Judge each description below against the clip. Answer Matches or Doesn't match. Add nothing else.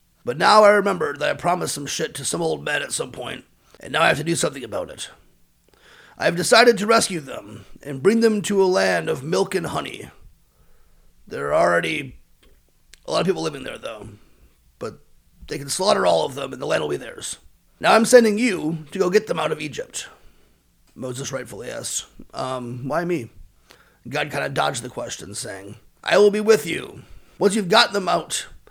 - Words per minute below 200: Doesn't match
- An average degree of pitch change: Doesn't match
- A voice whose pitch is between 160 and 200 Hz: Matches